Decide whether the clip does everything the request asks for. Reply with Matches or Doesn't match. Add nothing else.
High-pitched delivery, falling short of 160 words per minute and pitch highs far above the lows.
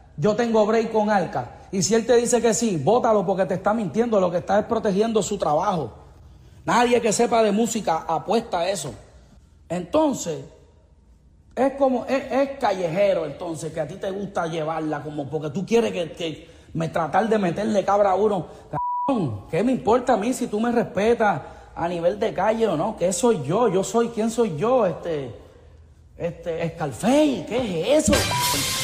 Doesn't match